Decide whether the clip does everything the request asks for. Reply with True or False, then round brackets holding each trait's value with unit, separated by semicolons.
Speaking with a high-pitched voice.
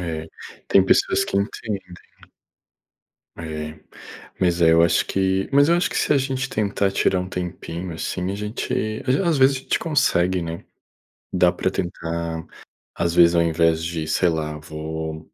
False (85 Hz)